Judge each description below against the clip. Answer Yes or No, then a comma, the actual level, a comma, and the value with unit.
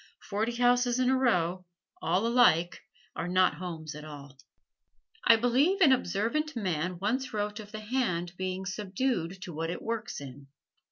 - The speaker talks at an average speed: Yes, average, 160 wpm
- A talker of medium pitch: No, high, 200 Hz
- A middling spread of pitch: No, wide, 5.9 semitones